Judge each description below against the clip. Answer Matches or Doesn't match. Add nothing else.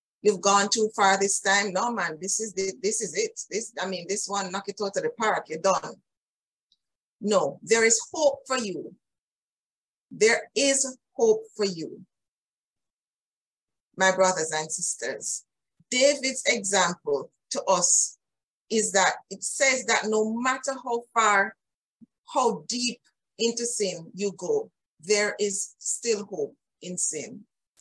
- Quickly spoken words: Doesn't match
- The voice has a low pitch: Doesn't match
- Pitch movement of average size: Matches